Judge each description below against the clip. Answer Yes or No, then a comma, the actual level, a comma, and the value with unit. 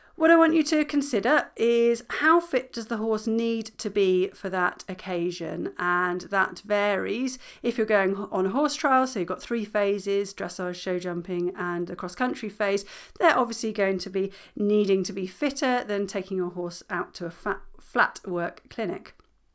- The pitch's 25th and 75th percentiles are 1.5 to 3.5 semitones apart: No, average, 4.3 semitones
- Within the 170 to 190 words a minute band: Yes, average, 185 wpm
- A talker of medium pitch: No, high, 200 Hz